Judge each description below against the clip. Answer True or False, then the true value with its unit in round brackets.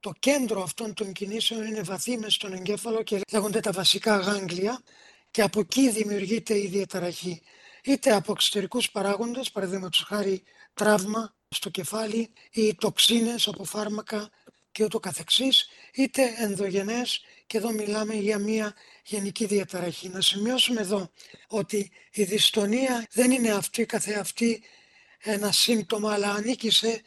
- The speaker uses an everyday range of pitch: False (2.1 semitones)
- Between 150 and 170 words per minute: False (135 wpm)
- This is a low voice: False (210 Hz)